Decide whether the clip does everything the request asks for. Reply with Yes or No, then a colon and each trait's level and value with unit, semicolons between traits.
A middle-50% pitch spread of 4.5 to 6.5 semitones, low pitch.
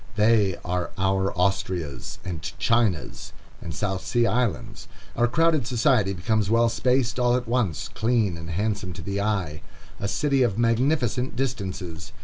Yes: average, 4.8 semitones; low, 110 Hz